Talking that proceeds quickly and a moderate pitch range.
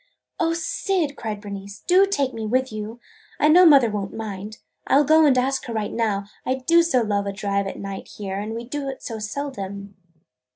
No: fast, 210 wpm; wide, 5.8 semitones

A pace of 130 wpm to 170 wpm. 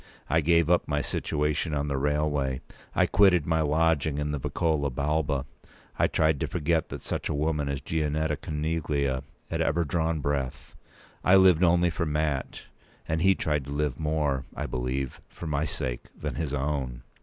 No: average, 180 wpm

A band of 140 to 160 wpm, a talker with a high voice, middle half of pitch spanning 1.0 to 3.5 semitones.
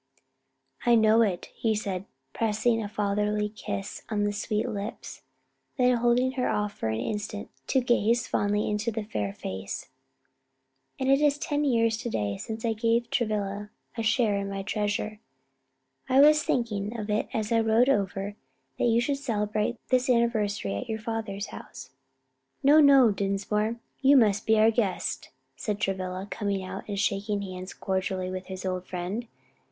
No: average, 170 wpm; high, 210 Hz; average, 2.9 semitones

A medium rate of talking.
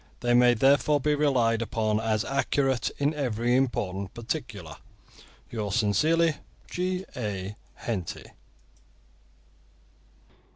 No: slow, 95 wpm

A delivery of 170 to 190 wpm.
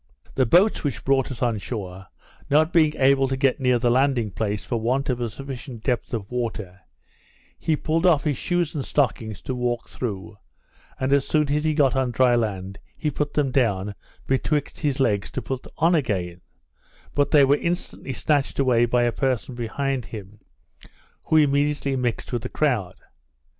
Yes: average, 180 wpm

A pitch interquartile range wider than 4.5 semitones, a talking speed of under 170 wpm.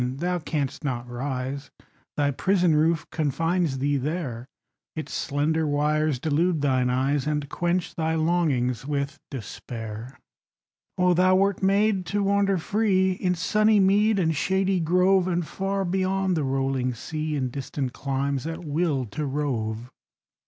Yes: average, 5.1 semitones; average, 140 wpm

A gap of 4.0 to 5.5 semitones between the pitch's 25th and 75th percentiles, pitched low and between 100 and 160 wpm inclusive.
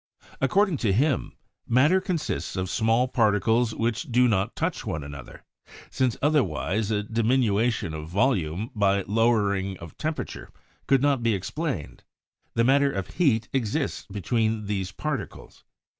Yes: average, 5.0 semitones; low, 115 Hz; average, 145 wpm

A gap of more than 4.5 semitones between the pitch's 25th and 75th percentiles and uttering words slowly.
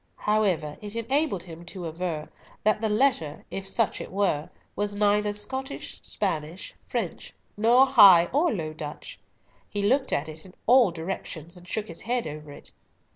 No: average, 5.1 semitones; average, 155 wpm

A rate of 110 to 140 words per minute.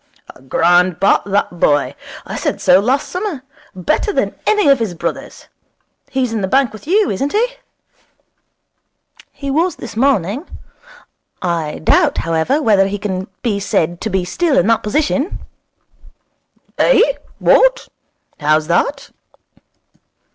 Yes: slow, 135 wpm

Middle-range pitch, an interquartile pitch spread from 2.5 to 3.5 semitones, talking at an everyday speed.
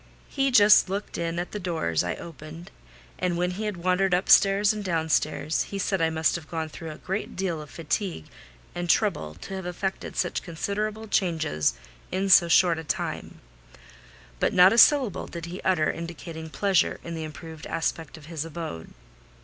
Yes: medium, 170 Hz; average, 3.1 semitones; average, 180 wpm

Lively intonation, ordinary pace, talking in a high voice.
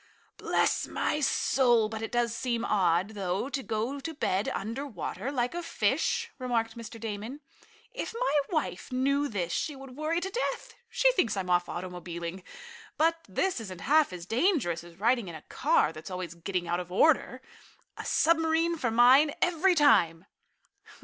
Yes: wide, 8.2 semitones; average, 170 wpm; high, 235 Hz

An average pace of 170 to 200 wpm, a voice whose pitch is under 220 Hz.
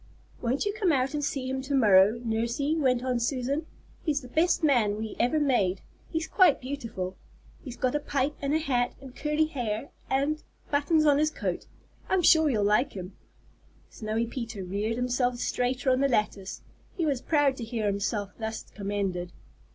No: average, 180 wpm; very high, 255 Hz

